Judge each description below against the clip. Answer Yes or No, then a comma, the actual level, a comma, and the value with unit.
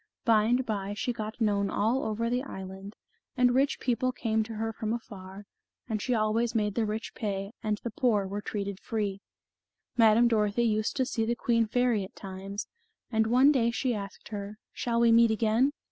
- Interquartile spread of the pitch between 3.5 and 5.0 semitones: No, narrow, 2.4 semitones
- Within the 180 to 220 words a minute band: Yes, average, 190 wpm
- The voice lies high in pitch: Yes, high, 220 Hz